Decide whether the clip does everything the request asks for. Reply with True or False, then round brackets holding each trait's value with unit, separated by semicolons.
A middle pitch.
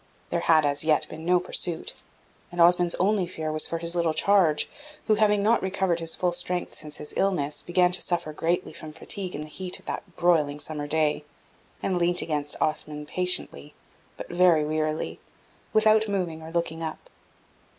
True (170 Hz)